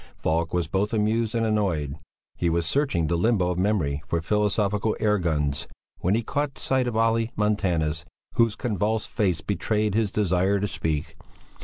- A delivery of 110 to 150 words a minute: No, average, 165 wpm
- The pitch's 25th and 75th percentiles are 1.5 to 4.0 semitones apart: No, average, 4.4 semitones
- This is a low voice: Yes, low, 100 Hz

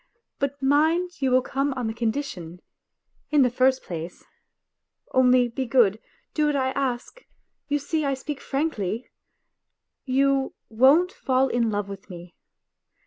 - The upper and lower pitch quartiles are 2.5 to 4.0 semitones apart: Yes, average, 3.5 semitones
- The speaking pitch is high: Yes, very high, 260 Hz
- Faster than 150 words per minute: No, average, 140 wpm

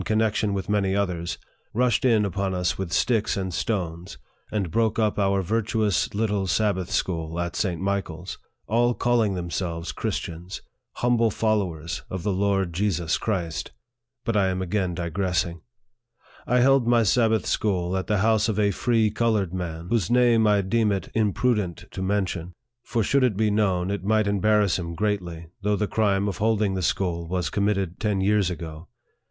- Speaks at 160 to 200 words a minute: Yes, average, 170 wpm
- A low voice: Yes, low, 100 Hz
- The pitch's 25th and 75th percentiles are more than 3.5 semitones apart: No, average, 3.2 semitones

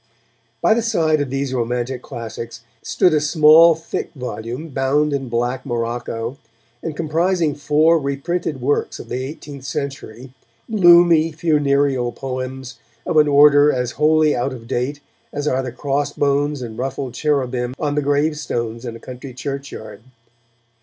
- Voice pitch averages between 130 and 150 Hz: Yes, medium, 140 Hz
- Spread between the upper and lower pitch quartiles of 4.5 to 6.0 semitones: No, average, 3.3 semitones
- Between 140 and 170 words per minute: Yes, average, 145 wpm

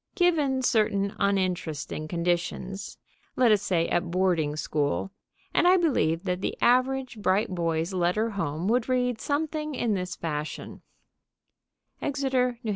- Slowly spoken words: Yes, slow, 130 wpm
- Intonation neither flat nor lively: No, wide, 6.6 semitones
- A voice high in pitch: Yes, high, 200 Hz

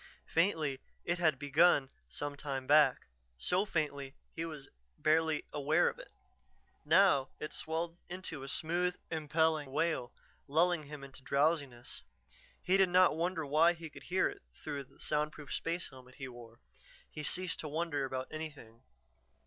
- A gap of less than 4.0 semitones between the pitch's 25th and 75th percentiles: Yes, average, 3.3 semitones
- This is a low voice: No, medium, 155 Hz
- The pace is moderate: Yes, average, 150 wpm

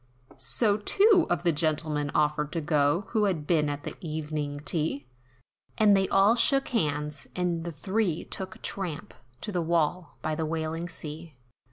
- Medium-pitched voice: Yes, medium, 165 Hz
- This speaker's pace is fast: No, average, 165 wpm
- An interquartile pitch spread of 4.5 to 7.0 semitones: No, average, 4.1 semitones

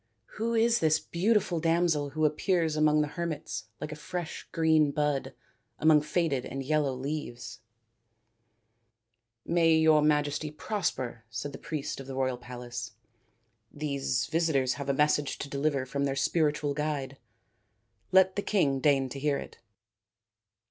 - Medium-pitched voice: Yes, medium, 145 Hz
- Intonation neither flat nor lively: Yes, average, 3.3 semitones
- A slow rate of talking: No, average, 155 wpm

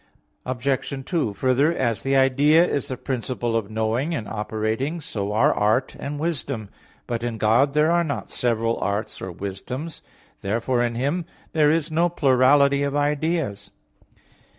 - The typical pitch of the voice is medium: No, low, 130 Hz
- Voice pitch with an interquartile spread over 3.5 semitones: Yes, average, 4.6 semitones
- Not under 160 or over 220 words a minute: No, average, 150 wpm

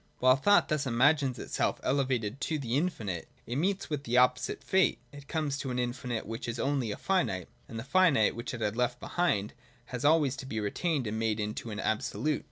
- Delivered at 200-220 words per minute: Yes, fast, 205 wpm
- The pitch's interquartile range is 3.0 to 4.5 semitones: Yes, average, 4.2 semitones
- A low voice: Yes, low, 125 Hz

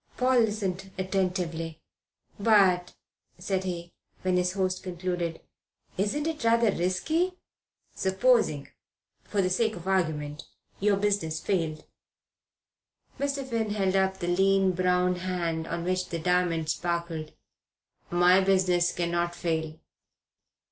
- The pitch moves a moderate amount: No, narrow, 2.3 semitones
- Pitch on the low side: No, medium, 185 Hz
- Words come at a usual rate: No, slow, 115 wpm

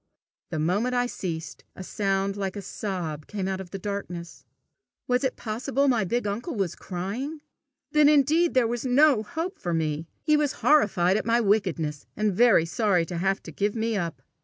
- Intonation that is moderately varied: No, wide, 5.7 semitones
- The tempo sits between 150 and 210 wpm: Yes, average, 185 wpm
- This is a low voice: No, high, 205 Hz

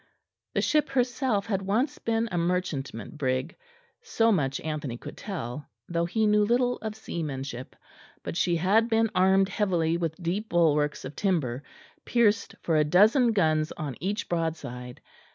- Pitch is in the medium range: Yes, medium, 175 Hz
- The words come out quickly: No, average, 155 wpm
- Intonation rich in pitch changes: Yes, wide, 6.1 semitones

